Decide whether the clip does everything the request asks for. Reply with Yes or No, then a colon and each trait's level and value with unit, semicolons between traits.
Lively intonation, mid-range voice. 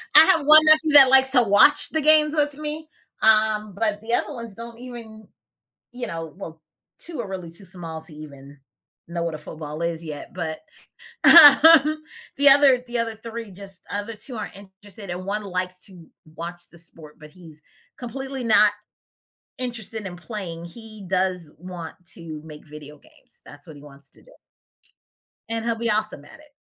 No: wide, 6.5 semitones; high, 205 Hz